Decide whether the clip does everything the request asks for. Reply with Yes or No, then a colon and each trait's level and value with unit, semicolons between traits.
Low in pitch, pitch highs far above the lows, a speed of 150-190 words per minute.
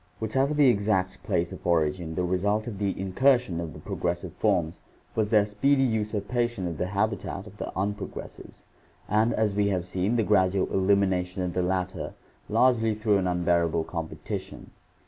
No: low, 100 Hz; average, 3.2 semitones; average, 165 wpm